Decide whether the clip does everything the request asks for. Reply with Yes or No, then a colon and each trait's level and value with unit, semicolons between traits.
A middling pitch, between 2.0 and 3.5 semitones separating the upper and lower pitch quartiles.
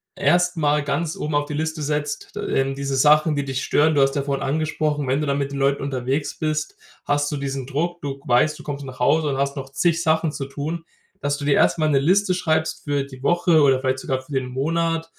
Yes: medium, 145 Hz; narrow, 2.4 semitones